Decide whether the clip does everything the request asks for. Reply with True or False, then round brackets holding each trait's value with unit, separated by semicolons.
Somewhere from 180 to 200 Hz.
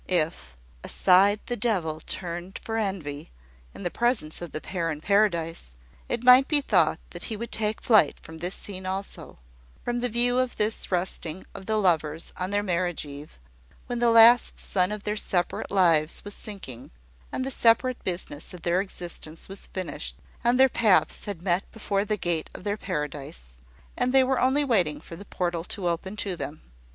True (190 Hz)